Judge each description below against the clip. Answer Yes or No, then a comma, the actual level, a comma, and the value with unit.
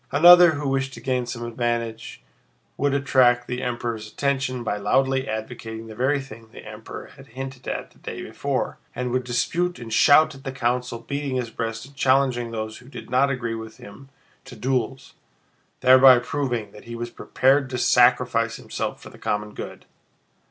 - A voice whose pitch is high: No, low, 125 Hz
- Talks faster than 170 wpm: Yes, average, 180 wpm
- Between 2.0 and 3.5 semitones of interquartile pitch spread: Yes, narrow, 2.6 semitones